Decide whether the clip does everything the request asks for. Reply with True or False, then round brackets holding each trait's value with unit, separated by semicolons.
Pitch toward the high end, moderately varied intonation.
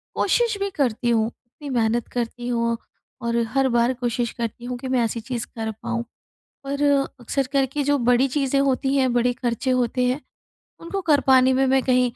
False (250 Hz; 2.3 semitones)